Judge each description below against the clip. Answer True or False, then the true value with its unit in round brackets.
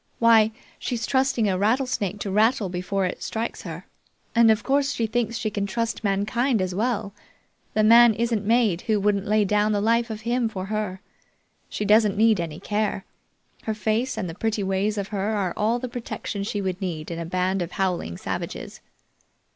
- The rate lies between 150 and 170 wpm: False (190 wpm)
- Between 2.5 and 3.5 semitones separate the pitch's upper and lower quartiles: True (2.9 semitones)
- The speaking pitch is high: True (210 Hz)